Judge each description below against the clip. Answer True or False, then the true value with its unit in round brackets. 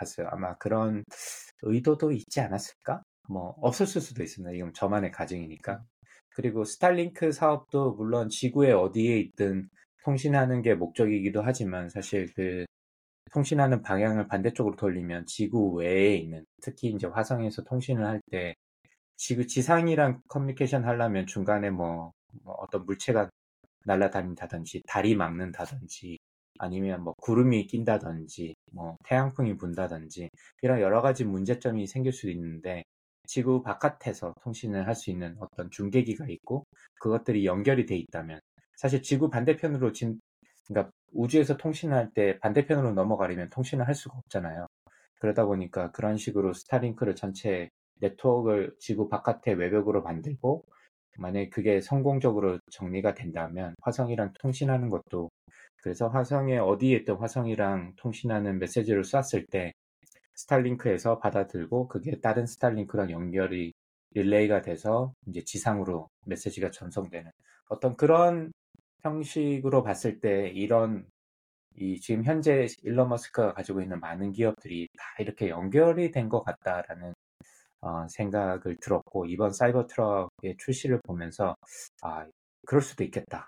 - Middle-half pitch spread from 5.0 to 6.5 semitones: True (5.6 semitones)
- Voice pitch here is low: True (105 Hz)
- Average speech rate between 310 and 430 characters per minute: True (330 characters per minute)